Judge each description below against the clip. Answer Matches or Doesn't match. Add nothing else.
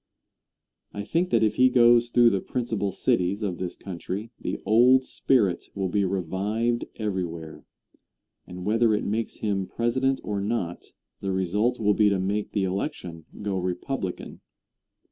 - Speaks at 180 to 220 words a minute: Doesn't match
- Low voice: Matches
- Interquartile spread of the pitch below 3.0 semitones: Doesn't match